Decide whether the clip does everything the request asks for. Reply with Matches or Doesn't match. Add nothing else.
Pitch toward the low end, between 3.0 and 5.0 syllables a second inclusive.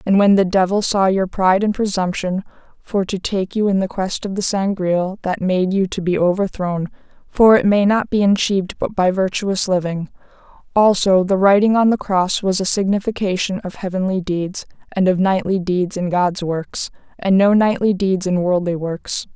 Doesn't match